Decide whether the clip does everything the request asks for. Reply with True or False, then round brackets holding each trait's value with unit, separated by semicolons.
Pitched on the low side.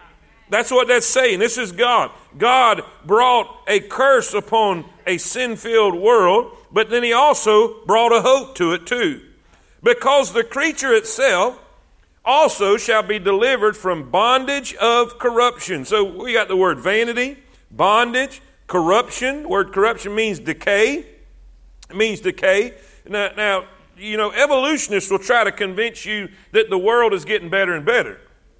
False (230 Hz)